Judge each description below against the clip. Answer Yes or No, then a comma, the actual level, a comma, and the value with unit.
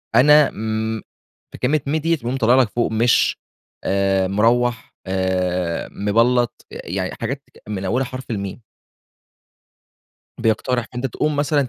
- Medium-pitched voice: No, low, 115 Hz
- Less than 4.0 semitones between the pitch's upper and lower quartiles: No, average, 4.5 semitones